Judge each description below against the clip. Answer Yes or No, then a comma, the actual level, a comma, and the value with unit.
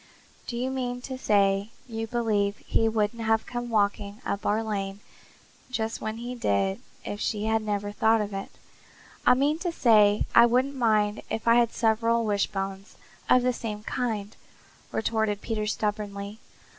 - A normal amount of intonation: No, narrow, 2.3 semitones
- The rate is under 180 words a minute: Yes, average, 165 wpm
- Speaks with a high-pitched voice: Yes, high, 220 Hz